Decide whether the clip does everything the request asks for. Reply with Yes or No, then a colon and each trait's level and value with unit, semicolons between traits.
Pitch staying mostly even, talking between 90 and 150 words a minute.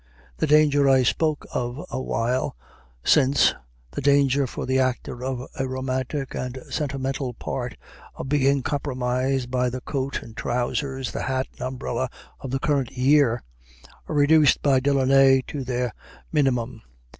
Yes: narrow, 1.8 semitones; average, 145 wpm